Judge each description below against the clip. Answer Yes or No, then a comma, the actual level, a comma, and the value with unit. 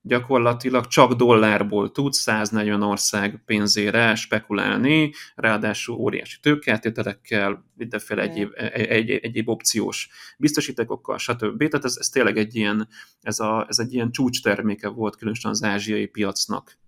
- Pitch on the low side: Yes, low, 110 Hz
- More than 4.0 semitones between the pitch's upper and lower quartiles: No, average, 2.8 semitones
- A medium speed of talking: Yes, average, 135 wpm